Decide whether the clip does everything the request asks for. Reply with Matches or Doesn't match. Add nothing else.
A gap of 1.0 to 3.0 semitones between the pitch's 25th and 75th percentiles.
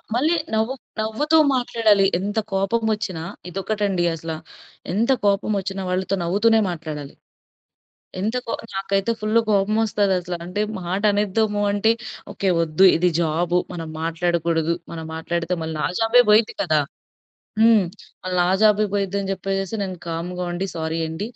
Doesn't match